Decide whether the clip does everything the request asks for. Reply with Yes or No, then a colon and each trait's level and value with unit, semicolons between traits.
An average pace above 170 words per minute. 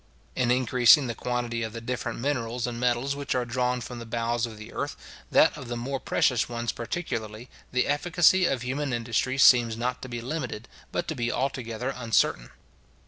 Yes: average, 190 wpm